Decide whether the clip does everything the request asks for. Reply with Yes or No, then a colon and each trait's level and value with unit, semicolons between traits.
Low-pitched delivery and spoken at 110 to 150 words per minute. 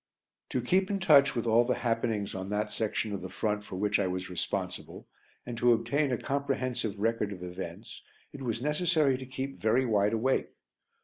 No: low, 115 Hz; average, 190 wpm